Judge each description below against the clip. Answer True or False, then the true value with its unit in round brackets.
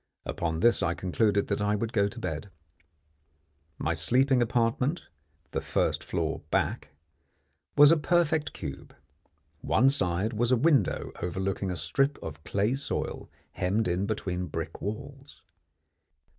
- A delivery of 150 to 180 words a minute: False (135 wpm)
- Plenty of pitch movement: True (6.5 semitones)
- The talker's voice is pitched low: True (105 Hz)